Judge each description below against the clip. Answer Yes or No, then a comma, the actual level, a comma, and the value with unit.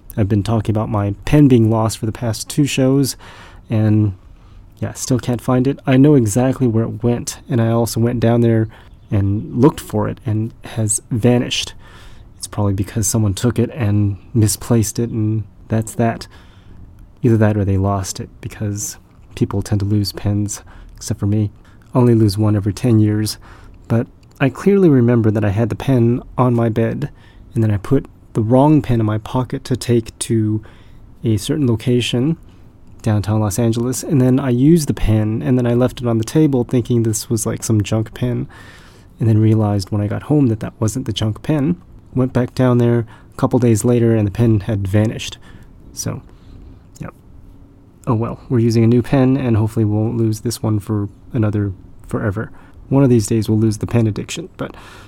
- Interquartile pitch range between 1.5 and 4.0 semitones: Yes, average, 2.8 semitones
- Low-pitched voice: Yes, low, 110 Hz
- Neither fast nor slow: Yes, average, 195 wpm